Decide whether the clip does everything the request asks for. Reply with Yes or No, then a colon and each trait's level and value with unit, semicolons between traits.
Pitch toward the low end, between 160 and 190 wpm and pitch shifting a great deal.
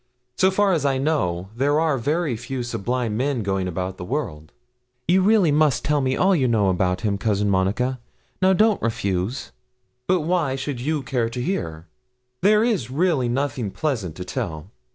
Yes: low, 130 Hz; average, 175 wpm; wide, 7.6 semitones